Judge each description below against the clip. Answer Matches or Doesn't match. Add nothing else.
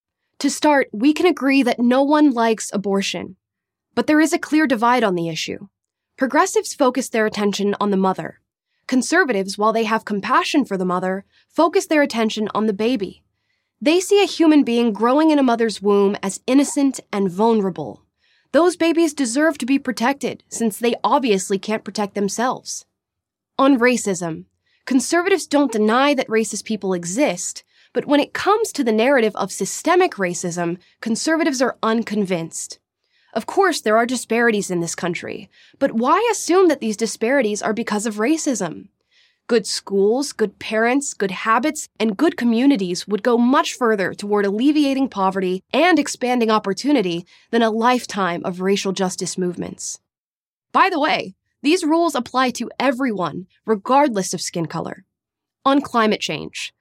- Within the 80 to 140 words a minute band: Doesn't match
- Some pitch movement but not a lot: Doesn't match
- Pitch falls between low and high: Doesn't match